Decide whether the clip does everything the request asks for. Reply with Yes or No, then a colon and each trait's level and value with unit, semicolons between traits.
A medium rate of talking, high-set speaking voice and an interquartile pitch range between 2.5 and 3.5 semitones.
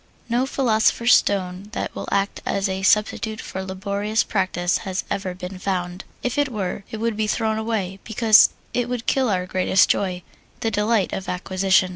Yes: average, 175 wpm; high, 200 Hz; average, 2.9 semitones